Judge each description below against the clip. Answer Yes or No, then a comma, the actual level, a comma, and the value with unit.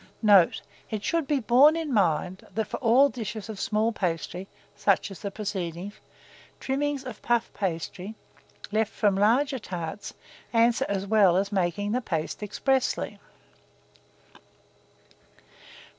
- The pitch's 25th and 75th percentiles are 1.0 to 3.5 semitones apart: No, average, 4.0 semitones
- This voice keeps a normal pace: No, slow, 130 wpm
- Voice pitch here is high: Yes, high, 210 Hz